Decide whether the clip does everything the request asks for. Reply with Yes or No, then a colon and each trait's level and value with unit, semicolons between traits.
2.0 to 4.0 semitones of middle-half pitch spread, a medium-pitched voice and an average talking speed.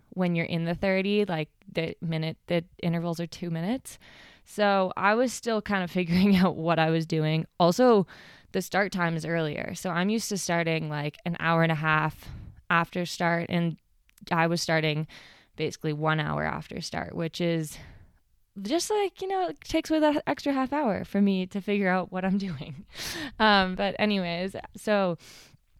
Yes: average, 3.7 semitones; medium, 175 Hz; average, 180 wpm